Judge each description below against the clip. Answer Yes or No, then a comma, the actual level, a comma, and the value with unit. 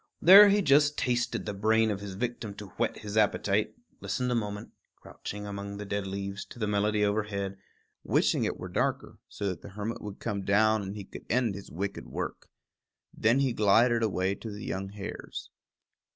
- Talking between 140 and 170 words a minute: No, average, 190 wpm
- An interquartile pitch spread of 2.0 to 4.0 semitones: Yes, narrow, 2.4 semitones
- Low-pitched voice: Yes, low, 105 Hz